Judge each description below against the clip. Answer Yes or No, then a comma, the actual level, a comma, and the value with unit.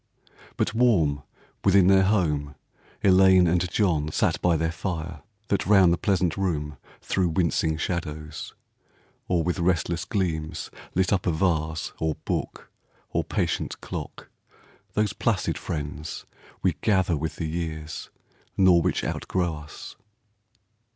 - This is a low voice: Yes, very low, 85 Hz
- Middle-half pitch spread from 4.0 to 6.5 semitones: No, average, 3.1 semitones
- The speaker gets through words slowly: Yes, slow, 130 wpm